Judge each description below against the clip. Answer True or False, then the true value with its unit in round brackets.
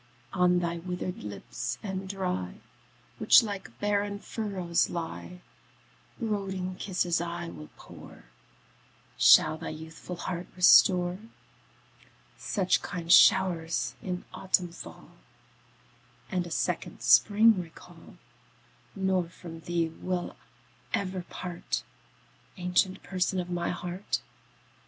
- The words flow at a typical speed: False (105 wpm)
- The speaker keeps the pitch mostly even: True (1.9 semitones)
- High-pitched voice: False (180 Hz)